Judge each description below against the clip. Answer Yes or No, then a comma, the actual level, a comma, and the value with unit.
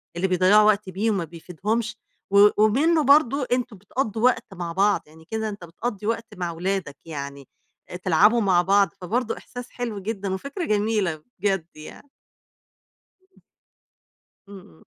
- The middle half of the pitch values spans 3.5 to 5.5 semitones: Yes, average, 4.1 semitones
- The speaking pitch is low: No, high, 205 Hz